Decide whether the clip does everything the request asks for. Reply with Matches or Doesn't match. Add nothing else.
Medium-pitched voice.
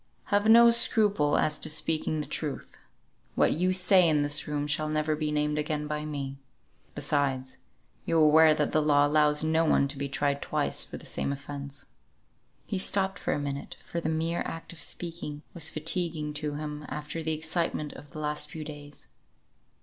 Matches